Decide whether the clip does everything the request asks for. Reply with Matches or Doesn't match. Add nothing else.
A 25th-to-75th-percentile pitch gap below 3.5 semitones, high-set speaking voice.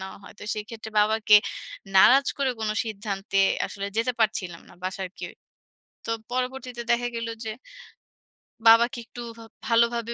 Matches